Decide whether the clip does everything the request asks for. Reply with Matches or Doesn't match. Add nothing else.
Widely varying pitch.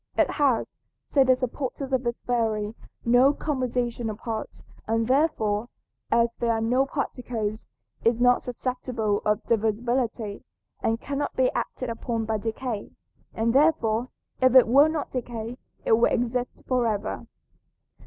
Doesn't match